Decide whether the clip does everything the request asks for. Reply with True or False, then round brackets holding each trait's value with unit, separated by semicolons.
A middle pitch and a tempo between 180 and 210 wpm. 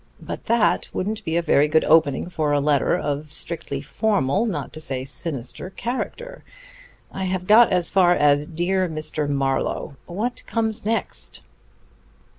False (170 Hz; 150 wpm)